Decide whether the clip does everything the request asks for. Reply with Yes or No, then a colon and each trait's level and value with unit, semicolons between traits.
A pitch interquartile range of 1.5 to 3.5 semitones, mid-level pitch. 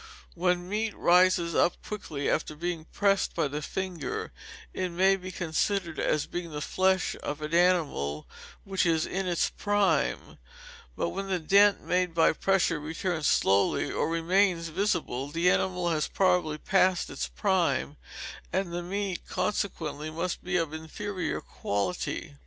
Yes: average, 3.1 semitones; medium, 175 Hz